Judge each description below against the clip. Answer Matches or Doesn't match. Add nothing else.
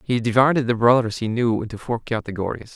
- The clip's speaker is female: Doesn't match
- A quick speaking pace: Doesn't match